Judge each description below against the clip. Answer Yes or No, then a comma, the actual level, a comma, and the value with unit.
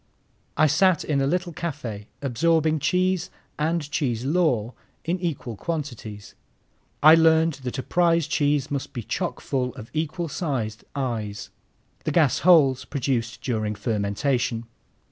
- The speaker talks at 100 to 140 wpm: Yes, slow, 135 wpm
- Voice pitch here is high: No, medium, 140 Hz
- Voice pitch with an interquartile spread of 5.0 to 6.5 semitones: Yes, wide, 5.5 semitones